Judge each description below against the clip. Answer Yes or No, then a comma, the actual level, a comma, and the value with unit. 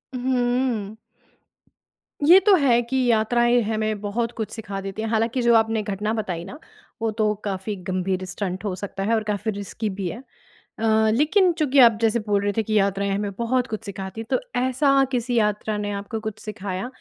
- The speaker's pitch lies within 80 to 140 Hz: No, high, 220 Hz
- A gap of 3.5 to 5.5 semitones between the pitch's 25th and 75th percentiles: No, average, 2.9 semitones